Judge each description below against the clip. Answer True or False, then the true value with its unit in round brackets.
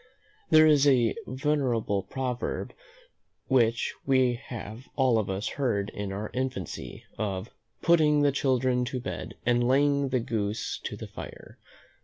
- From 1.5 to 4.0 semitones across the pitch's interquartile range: True (3.5 semitones)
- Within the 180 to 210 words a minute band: False (140 wpm)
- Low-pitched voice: True (125 Hz)